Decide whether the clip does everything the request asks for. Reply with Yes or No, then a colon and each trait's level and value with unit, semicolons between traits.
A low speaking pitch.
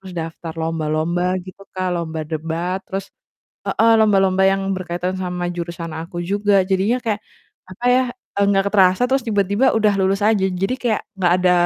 No: high, 190 Hz